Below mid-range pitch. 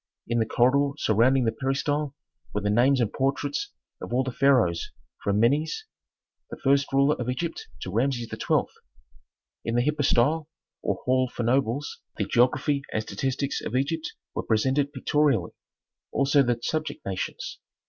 Yes: low, 130 Hz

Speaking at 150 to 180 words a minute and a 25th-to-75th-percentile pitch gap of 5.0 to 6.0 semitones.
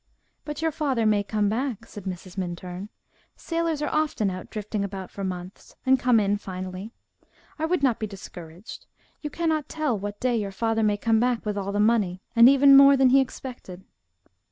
No: average, 190 wpm; average, 5.3 semitones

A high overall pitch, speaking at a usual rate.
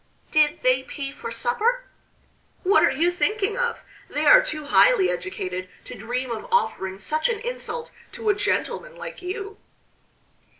Yes: very high, 370 Hz; average, 155 wpm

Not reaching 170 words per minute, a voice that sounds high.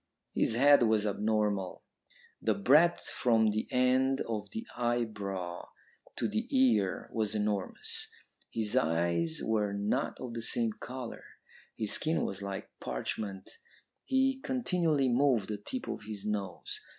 No: slow, 135 wpm; low, 110 Hz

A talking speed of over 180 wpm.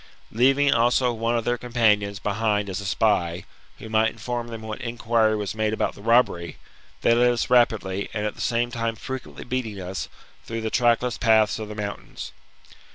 Yes: average, 190 wpm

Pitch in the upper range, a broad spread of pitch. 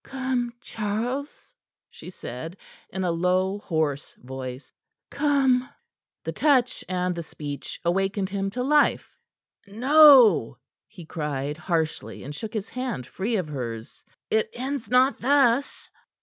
Yes: high, 195 Hz; wide, 7.9 semitones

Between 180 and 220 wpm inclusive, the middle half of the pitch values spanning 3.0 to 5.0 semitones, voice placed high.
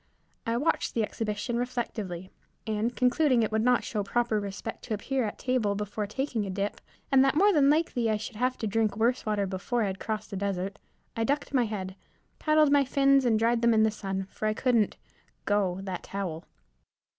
Yes: fast, 205 wpm; average, 3.7 semitones; high, 220 Hz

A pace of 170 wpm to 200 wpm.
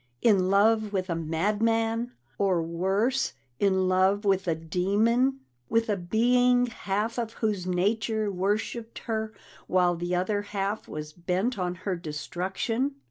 No: slow, 135 wpm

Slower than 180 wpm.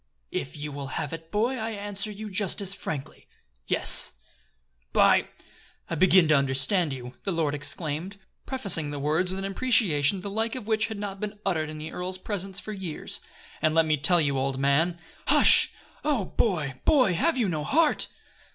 No: average, 190 wpm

